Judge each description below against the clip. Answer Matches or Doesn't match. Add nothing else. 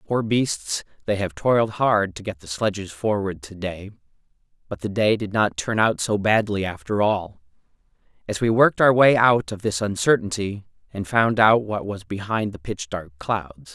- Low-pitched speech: Matches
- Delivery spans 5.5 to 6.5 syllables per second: Doesn't match